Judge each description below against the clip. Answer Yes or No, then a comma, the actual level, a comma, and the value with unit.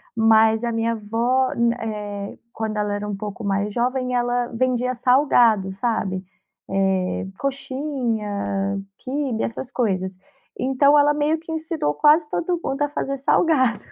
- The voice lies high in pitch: Yes, high, 235 Hz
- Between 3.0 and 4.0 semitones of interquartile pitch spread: No, average, 4.5 semitones